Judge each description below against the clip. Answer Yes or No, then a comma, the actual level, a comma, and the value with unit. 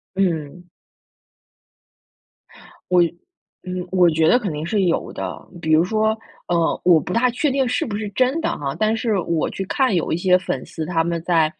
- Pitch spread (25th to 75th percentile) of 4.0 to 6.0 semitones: Yes, average, 4.8 semitones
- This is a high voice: No, medium, 180 Hz